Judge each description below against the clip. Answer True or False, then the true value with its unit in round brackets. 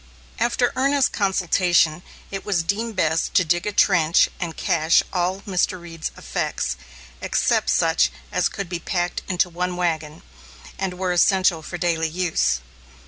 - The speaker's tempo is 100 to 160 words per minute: True (145 wpm)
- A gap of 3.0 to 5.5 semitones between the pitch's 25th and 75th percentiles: False (2.6 semitones)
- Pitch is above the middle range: False (180 Hz)